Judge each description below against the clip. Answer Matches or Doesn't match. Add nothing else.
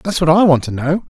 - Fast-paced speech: Matches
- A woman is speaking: Doesn't match